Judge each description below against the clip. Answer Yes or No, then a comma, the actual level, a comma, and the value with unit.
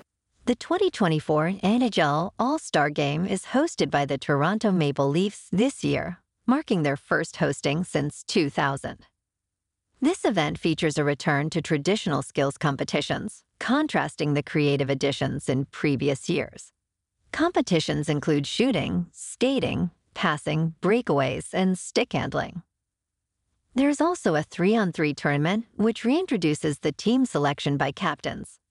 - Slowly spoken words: Yes, slow, 130 wpm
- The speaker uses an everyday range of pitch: No, wide, 6.9 semitones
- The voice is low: No, medium, 155 Hz